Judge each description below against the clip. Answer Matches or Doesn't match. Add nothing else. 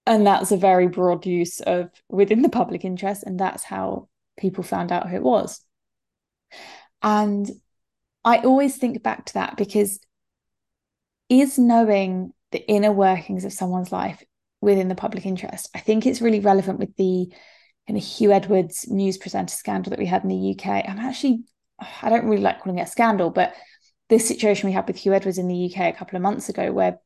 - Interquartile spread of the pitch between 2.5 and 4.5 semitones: Matches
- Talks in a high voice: Matches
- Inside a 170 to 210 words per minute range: Matches